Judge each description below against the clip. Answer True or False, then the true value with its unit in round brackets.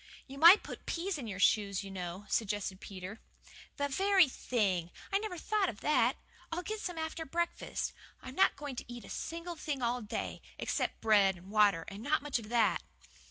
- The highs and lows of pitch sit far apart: True (8.4 semitones)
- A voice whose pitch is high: True (245 Hz)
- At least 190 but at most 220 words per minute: True (195 wpm)